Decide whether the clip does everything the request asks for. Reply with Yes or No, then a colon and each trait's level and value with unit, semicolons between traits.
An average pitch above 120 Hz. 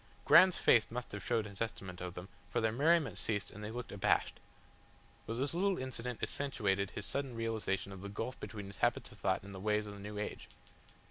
No: low, 110 Hz